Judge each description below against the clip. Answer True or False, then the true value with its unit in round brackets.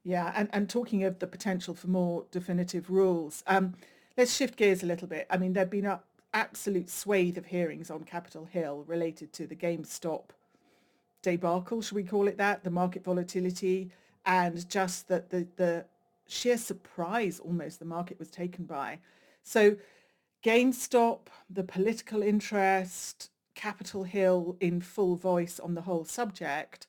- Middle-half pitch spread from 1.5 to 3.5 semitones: True (2.6 semitones)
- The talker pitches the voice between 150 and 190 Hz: True (185 Hz)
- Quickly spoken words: False (160 wpm)